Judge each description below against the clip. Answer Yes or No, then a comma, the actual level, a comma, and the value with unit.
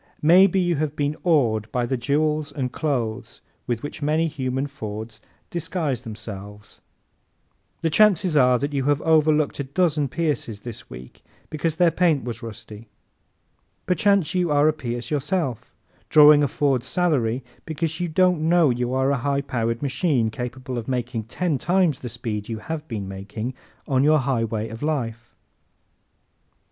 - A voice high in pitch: No, medium, 140 Hz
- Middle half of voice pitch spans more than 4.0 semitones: Yes, average, 4.9 semitones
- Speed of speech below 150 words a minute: No, average, 155 wpm